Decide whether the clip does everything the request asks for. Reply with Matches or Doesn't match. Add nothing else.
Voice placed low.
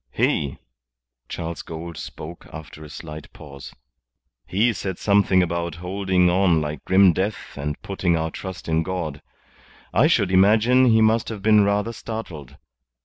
Matches